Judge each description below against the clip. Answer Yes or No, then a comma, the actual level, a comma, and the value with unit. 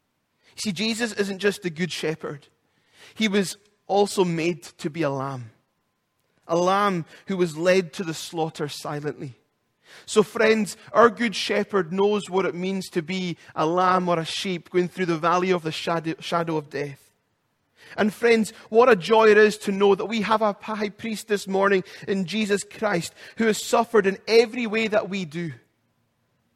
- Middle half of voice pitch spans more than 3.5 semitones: Yes, average, 4.3 semitones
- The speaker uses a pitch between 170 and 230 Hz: Yes, high, 190 Hz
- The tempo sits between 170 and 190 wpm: Yes, average, 175 wpm